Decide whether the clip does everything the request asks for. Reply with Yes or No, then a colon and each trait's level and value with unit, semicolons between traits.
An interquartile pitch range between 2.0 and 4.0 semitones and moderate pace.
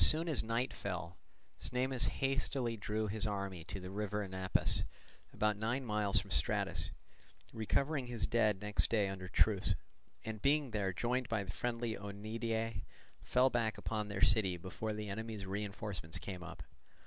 Yes: average, 2.9 semitones; average, 160 wpm